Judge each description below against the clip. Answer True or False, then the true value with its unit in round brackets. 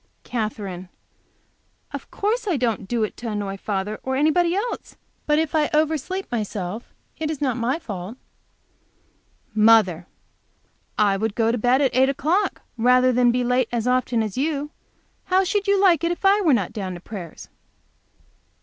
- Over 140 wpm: True (170 wpm)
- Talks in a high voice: True (250 Hz)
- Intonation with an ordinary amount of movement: False (6.6 semitones)